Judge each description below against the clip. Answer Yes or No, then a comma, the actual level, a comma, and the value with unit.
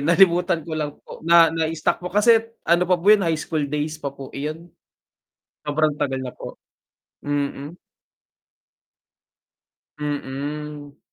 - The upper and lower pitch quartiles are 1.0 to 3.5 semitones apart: Yes, average, 2.7 semitones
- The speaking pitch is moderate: Yes, medium, 155 Hz